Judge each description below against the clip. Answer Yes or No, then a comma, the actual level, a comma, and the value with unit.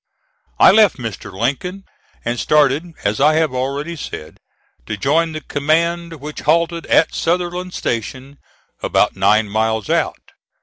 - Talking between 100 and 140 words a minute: Yes, slow, 135 wpm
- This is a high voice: No, medium, 150 Hz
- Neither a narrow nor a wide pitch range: No, wide, 5.8 semitones